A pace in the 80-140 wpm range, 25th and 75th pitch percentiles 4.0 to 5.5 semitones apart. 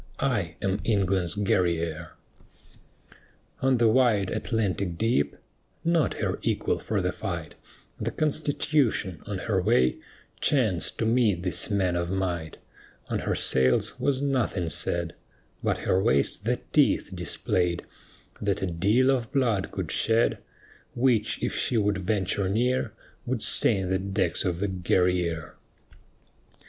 Yes: slow, 135 wpm; average, 4.7 semitones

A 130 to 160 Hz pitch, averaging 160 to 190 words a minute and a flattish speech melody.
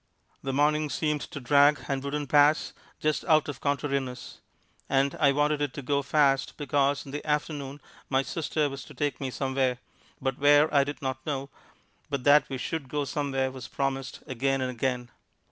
Yes: medium, 140 Hz; average, 180 wpm; narrow, 1.7 semitones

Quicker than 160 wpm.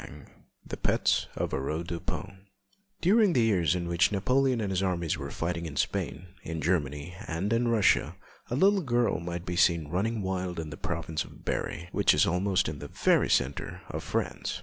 Yes: average, 190 wpm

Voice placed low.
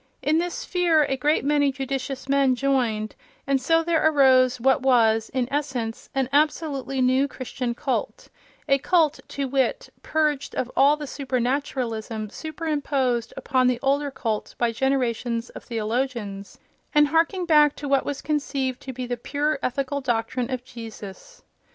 No: very high, 270 Hz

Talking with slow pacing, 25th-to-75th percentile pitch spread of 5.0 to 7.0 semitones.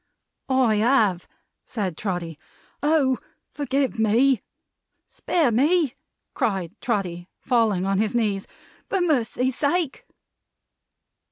Yes: slow, 95 wpm; wide, 5.6 semitones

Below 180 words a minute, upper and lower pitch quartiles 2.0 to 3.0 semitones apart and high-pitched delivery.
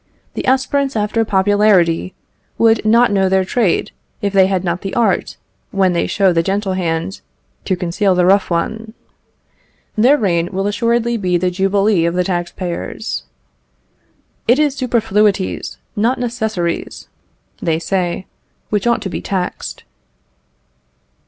No: average, 140 wpm; average, 3.6 semitones; high, 195 Hz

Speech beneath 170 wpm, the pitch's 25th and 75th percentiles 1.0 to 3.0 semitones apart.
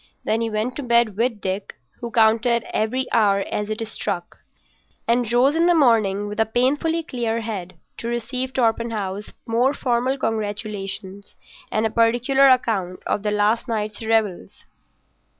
Yes: average, 150 wpm; average, 2.7 semitones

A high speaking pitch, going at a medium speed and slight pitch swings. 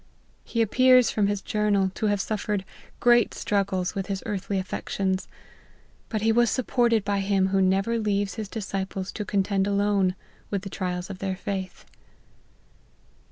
Yes: high, 200 Hz; average, 160 wpm; narrow, 1.8 semitones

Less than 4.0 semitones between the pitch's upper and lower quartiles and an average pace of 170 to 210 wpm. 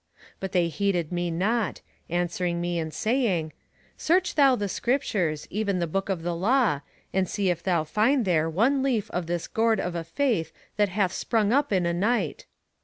No: average, 4.6 semitones; average, 185 wpm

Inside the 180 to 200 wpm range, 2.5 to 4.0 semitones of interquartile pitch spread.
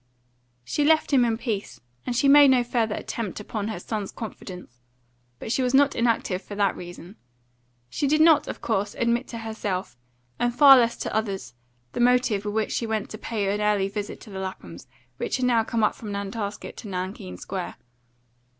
Yes: average, 195 wpm; average, 3.5 semitones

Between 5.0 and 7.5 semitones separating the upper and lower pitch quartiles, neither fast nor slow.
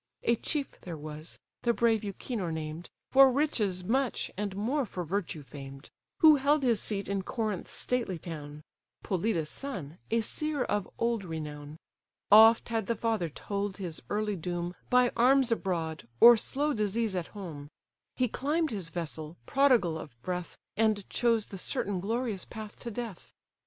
Yes: wide, 5.5 semitones; average, 155 wpm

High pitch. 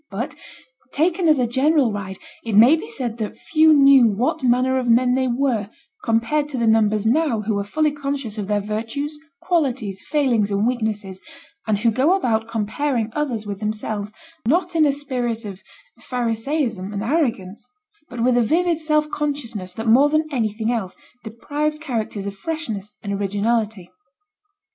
Yes: high, 235 Hz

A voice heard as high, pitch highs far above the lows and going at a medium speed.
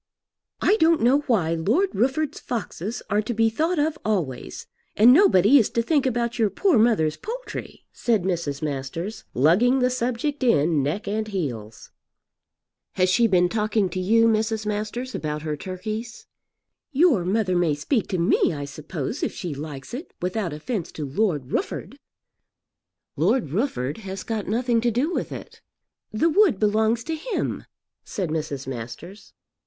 Yes: high, 215 Hz; wide, 6.8 semitones; average, 160 wpm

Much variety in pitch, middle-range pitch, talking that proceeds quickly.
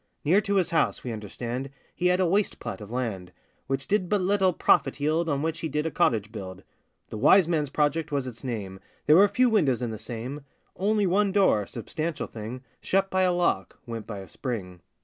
Yes: wide, 8.1 semitones; medium, 145 Hz; fast, 210 wpm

